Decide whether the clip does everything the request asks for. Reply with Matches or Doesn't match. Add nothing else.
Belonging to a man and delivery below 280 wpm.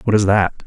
Matches